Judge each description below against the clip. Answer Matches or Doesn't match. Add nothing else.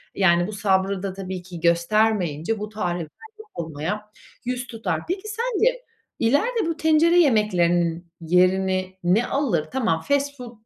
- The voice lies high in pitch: Matches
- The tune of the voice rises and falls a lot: Matches